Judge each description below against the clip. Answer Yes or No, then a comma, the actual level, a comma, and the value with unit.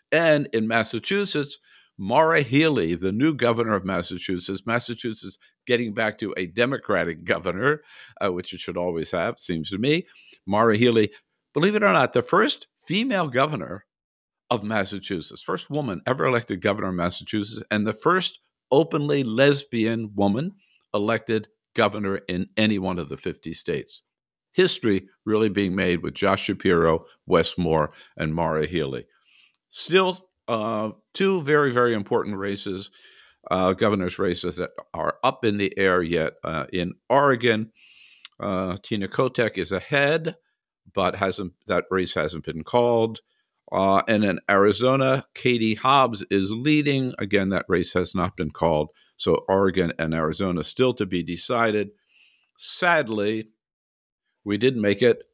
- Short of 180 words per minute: Yes, average, 145 wpm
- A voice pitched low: Yes, low, 105 Hz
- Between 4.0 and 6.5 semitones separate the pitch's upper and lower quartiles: Yes, average, 4.4 semitones